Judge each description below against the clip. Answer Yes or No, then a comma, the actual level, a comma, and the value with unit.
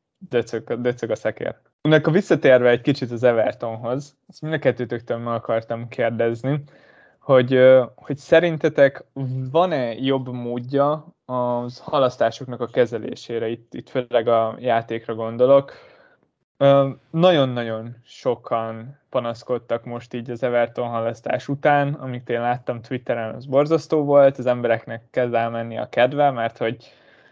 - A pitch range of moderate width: Yes, average, 3.2 semitones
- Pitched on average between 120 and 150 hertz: Yes, low, 125 Hz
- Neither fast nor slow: Yes, average, 120 wpm